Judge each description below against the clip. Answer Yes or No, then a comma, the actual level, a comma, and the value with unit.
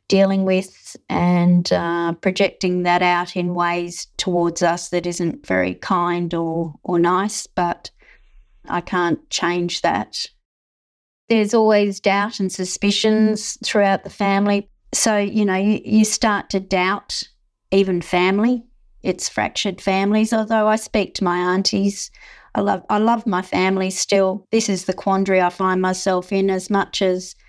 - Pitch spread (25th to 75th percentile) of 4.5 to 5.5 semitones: No, narrow, 2.6 semitones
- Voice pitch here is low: No, high, 190 Hz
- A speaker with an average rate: Yes, average, 150 wpm